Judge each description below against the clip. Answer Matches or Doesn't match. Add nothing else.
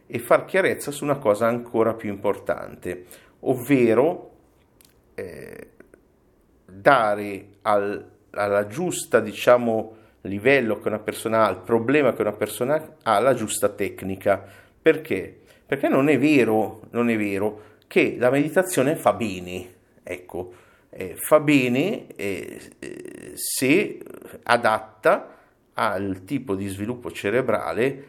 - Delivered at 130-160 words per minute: Doesn't match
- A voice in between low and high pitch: Doesn't match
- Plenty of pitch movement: Doesn't match